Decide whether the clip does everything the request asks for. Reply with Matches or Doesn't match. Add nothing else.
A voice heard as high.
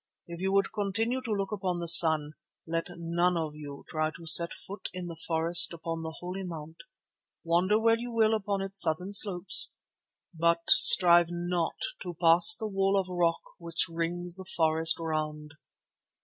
Doesn't match